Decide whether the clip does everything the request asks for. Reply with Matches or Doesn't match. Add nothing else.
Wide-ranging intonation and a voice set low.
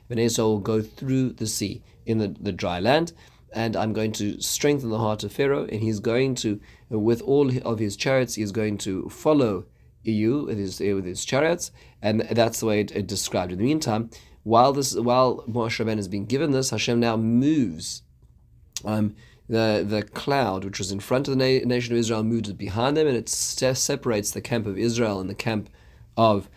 Doesn't match